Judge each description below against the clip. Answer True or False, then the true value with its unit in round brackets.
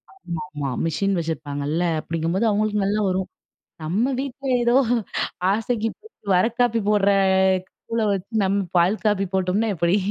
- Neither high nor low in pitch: False (195 Hz)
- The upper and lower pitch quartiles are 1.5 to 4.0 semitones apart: False (4.4 semitones)